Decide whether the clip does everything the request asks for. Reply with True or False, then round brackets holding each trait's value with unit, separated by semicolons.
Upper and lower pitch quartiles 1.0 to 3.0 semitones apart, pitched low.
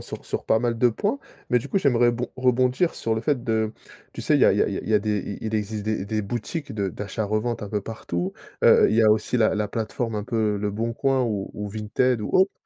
True (2.5 semitones; 110 Hz)